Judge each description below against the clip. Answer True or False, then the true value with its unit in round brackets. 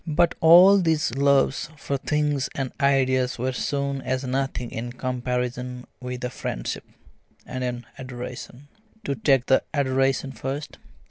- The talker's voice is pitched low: True (130 Hz)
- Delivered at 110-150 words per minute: True (135 wpm)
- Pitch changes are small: True (1.9 semitones)